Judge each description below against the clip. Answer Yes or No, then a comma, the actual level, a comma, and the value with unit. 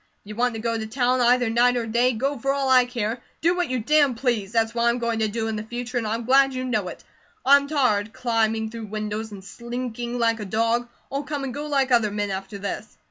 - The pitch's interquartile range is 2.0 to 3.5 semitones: Yes, narrow, 2.6 semitones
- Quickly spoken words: Yes, fast, 255 wpm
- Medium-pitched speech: No, high, 235 Hz